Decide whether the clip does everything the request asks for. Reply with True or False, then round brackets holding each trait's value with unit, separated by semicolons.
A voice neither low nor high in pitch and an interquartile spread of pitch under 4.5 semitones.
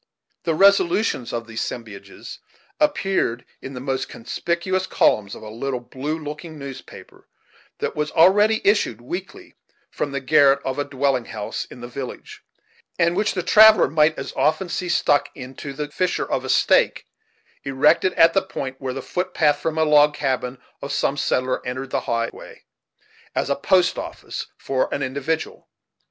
False (145 Hz; 4.8 semitones)